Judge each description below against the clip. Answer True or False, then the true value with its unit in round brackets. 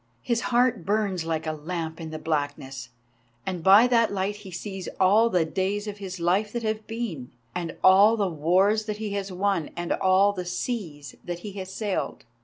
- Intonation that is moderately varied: True (3.7 semitones)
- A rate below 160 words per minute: False (195 wpm)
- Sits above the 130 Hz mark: True (190 Hz)